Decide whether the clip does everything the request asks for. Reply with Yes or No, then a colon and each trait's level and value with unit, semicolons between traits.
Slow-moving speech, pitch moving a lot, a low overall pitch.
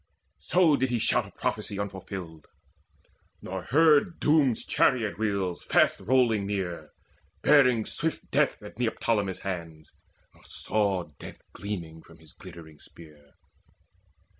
Yes: slow, 120 wpm; wide, 6.5 semitones; low, 100 Hz